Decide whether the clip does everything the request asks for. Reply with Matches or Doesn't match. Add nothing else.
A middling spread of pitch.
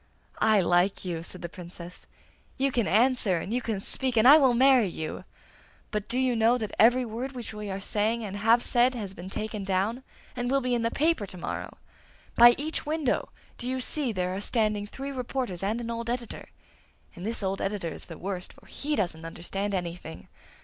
Matches